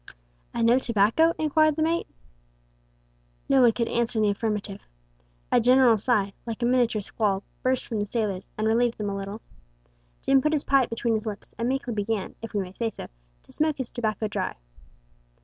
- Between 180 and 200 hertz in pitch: No, high, 230 Hz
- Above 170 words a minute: Yes, average, 190 wpm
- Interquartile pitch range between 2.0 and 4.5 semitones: Yes, average, 3.4 semitones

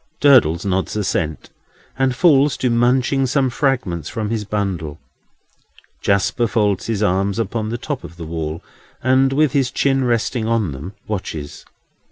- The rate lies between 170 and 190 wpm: No, average, 150 wpm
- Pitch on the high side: No, low, 110 Hz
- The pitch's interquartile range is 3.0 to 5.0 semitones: No, wide, 5.5 semitones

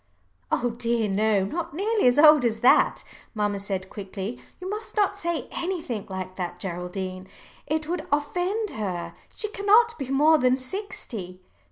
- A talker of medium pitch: No, very high, 250 Hz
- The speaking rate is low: No, average, 155 wpm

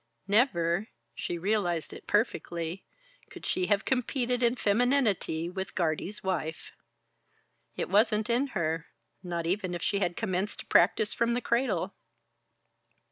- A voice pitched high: Yes, high, 200 Hz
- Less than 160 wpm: Yes, slow, 135 wpm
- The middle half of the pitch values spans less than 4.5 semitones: No, average, 5.0 semitones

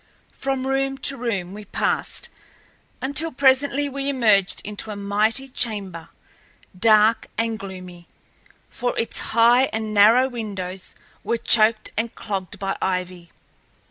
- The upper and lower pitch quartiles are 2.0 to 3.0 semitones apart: No, average, 4.7 semitones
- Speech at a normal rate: No, slow, 125 wpm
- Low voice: No, high, 220 Hz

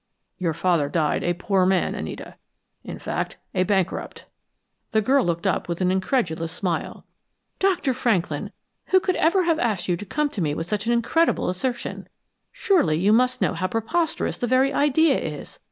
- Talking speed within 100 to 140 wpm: No, average, 175 wpm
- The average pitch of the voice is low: No, high, 210 Hz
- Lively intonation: Yes, wide, 7.4 semitones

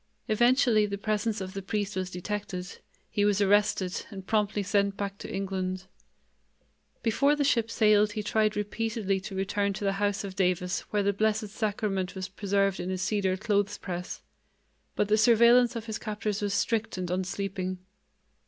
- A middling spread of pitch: No, narrow, 2.0 semitones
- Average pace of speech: Yes, average, 170 wpm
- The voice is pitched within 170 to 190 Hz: No, high, 205 Hz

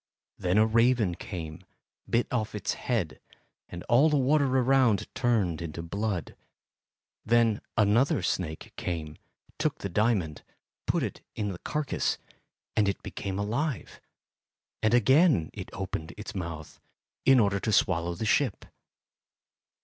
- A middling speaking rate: No, slow, 130 wpm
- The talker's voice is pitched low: Yes, low, 105 Hz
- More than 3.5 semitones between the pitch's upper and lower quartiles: Yes, wide, 5.4 semitones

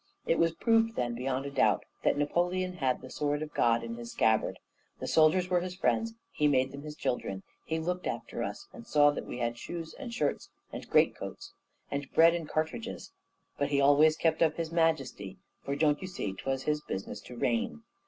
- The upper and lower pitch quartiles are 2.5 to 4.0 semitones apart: No, average, 4.5 semitones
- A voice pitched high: No, medium, 150 Hz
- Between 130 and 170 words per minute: No, fast, 205 wpm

